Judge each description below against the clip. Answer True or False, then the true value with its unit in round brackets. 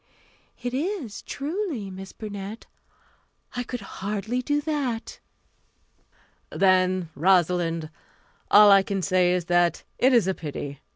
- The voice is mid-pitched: False (195 Hz)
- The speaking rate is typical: False (120 wpm)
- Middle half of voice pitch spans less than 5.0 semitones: False (5.3 semitones)